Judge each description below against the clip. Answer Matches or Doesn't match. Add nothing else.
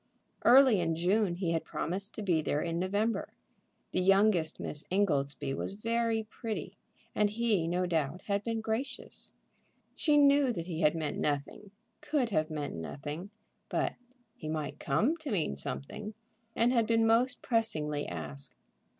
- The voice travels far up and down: Matches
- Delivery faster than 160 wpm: Doesn't match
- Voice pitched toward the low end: Doesn't match